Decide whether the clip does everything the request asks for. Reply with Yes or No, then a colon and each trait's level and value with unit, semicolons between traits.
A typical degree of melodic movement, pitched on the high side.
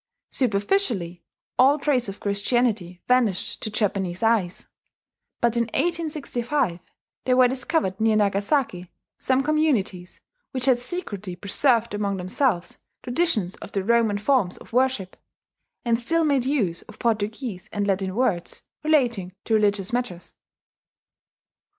Yes: average, 4.8 semitones; high, 225 Hz